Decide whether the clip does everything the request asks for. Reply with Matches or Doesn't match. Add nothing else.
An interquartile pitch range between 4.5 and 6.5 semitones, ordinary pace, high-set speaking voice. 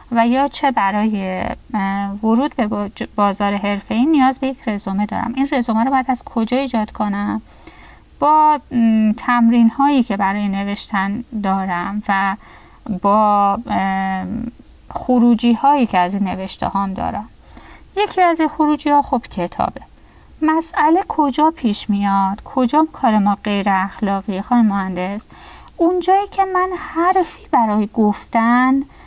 Matches